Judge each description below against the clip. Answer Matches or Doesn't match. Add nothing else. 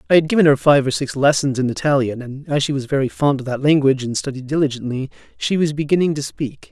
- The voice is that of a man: Matches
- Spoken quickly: Matches